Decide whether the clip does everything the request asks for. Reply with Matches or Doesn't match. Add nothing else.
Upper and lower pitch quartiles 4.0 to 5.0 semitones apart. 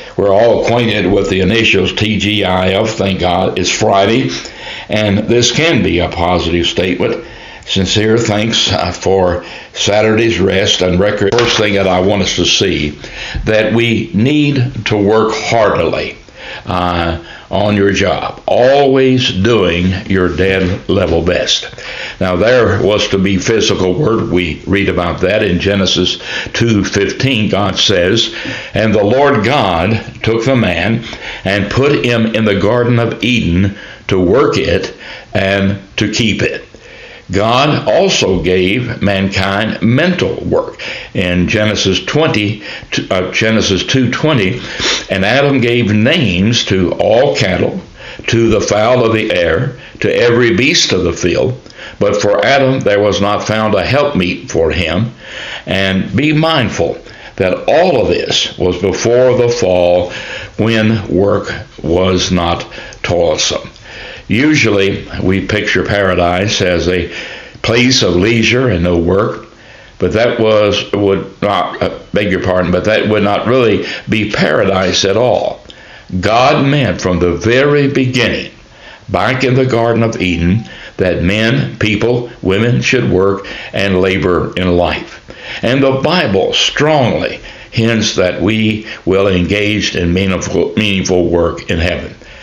Doesn't match